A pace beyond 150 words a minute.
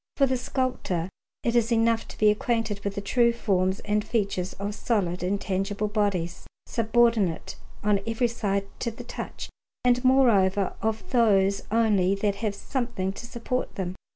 Yes: average, 160 wpm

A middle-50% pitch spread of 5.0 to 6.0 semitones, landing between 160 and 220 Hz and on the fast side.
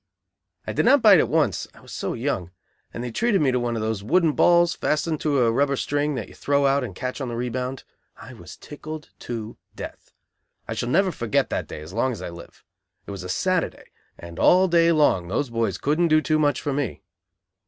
No: average, 5.3 semitones; low, 135 Hz; fast, 225 wpm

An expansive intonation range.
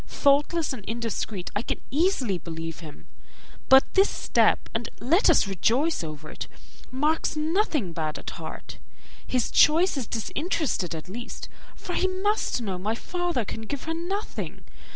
Yes: wide, 9.0 semitones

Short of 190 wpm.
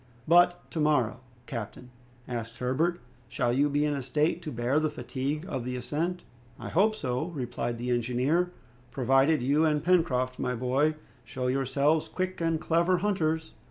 Yes: average, 160 wpm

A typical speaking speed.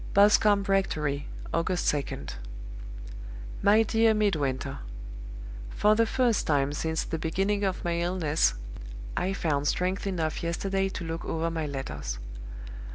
No: slow, 125 wpm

